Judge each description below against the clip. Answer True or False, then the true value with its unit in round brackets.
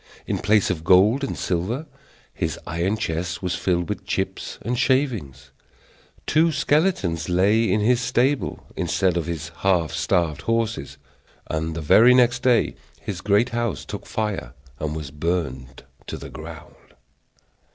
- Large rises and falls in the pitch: True (6.2 semitones)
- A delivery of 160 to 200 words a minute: False (145 wpm)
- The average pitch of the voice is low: True (95 Hz)